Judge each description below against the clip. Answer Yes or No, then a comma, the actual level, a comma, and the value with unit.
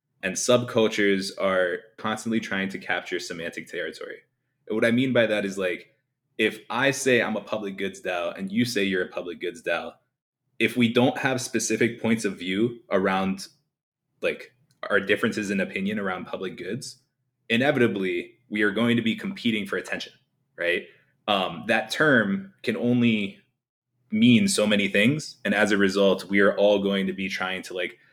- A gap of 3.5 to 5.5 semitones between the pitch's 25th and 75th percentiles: Yes, average, 4.4 semitones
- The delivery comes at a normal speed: Yes, average, 175 wpm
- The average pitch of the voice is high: No, low, 115 Hz